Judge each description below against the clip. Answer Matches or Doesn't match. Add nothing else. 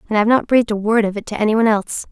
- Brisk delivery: Matches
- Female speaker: Matches